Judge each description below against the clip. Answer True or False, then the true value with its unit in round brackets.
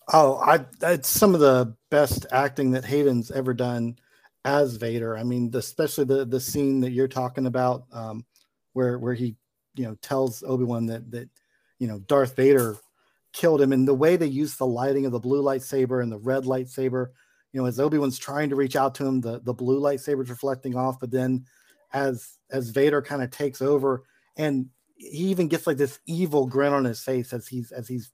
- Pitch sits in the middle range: False (130 Hz)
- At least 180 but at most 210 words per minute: True (205 wpm)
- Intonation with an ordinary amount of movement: False (2.0 semitones)